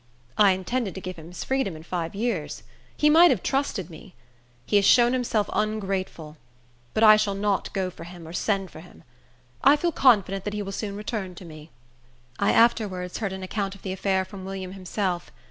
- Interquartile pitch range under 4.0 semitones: Yes, average, 2.8 semitones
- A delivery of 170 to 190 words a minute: No, average, 200 wpm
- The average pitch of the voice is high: Yes, high, 195 Hz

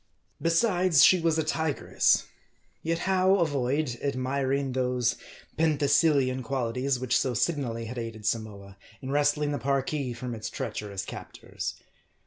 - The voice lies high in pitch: No, low, 135 Hz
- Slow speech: Yes, slow, 125 wpm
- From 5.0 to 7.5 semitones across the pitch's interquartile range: No, average, 4.1 semitones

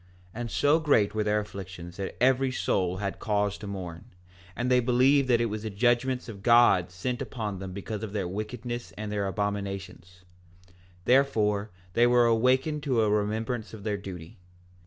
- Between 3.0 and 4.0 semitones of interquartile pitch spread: Yes, average, 3.6 semitones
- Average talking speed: Yes, average, 180 wpm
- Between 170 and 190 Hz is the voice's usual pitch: No, low, 105 Hz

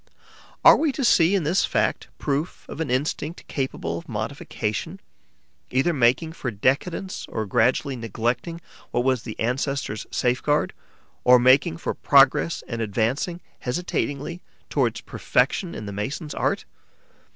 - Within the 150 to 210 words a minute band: No, slow, 135 wpm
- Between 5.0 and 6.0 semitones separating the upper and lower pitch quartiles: Yes, wide, 5.5 semitones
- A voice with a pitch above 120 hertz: Yes, low, 135 Hz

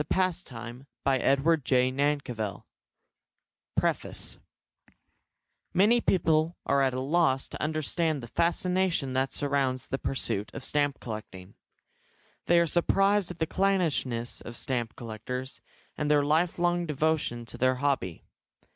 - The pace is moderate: No, slow, 125 wpm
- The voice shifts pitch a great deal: No, average, 4.7 semitones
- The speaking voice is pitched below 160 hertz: Yes, medium, 140 Hz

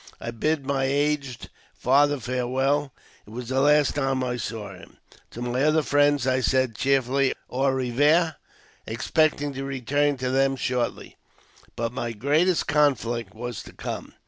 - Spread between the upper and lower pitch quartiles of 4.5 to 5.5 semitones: No, average, 2.8 semitones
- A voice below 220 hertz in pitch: Yes, low, 135 Hz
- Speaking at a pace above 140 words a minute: Yes, average, 160 wpm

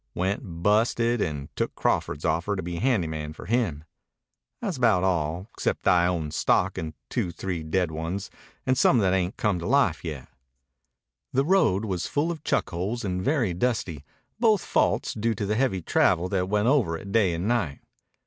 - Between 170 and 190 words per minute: Yes, average, 185 wpm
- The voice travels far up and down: Yes, wide, 5.7 semitones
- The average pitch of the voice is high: No, very low, 95 Hz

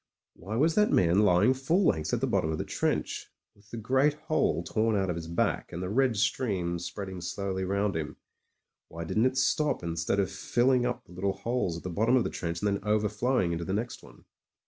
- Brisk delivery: Yes, fast, 220 wpm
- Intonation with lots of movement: Yes, wide, 5.9 semitones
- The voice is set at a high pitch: No, low, 100 Hz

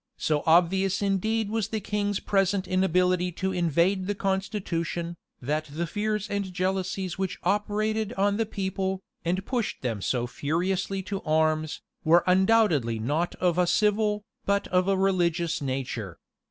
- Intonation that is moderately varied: Yes, average, 3.1 semitones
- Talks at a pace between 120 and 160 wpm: Yes, average, 145 wpm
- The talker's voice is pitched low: No, medium, 185 Hz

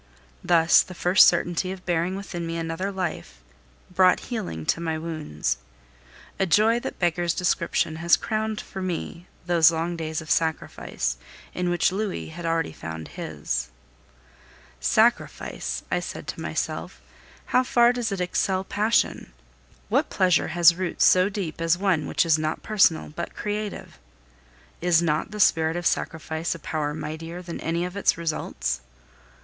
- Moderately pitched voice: Yes, medium, 170 Hz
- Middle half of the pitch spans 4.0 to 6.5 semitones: No, average, 2.8 semitones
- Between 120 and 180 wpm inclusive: Yes, average, 155 wpm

